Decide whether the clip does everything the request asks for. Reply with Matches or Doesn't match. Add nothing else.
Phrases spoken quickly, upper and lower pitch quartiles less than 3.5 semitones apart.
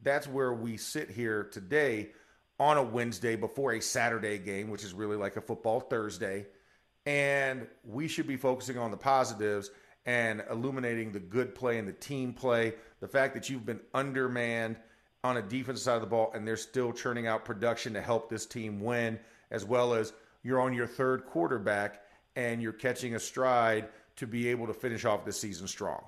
Doesn't match